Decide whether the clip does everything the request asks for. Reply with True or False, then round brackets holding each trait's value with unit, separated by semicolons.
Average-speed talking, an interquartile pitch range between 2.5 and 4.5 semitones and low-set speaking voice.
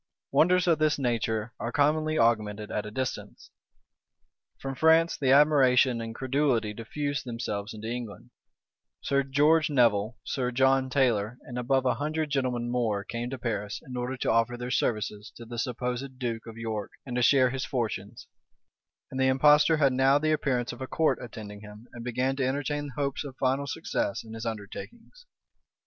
True (175 wpm; 3.4 semitones; 125 Hz)